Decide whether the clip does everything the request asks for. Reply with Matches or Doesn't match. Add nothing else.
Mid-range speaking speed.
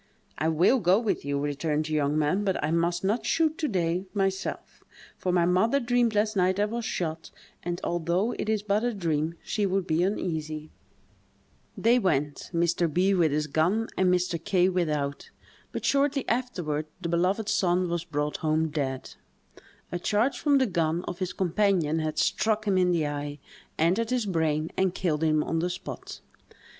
Matches